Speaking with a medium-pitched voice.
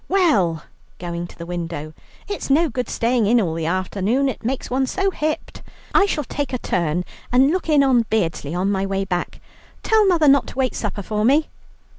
No: high, 230 Hz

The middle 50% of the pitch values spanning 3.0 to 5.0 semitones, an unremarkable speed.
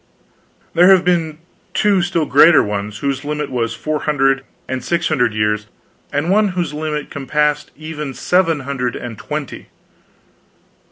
Yes: average, 4.1 semitones; average, 145 wpm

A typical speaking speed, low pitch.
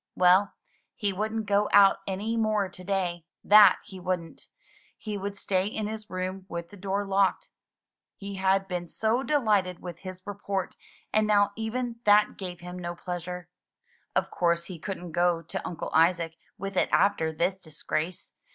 No: average, 165 wpm; high, 190 Hz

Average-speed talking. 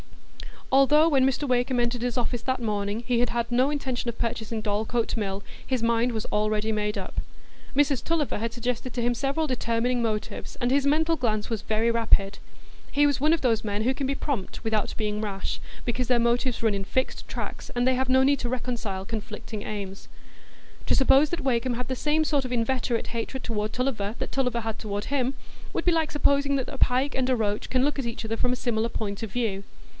No: fast, 215 wpm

